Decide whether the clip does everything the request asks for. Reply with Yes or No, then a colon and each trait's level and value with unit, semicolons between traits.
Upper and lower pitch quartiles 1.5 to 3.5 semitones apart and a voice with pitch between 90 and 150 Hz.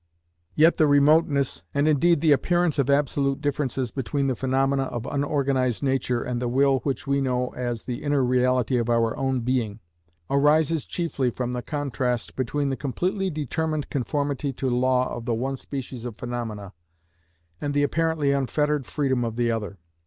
Yes: average, 2.7 semitones; low, 135 Hz